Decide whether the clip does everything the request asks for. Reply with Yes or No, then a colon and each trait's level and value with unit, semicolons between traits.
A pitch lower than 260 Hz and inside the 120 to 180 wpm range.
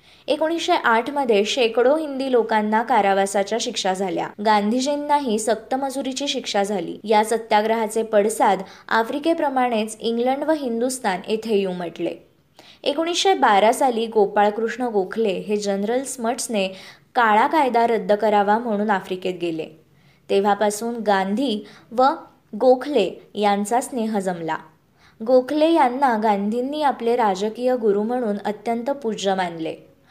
No: high, 225 Hz; average, 105 wpm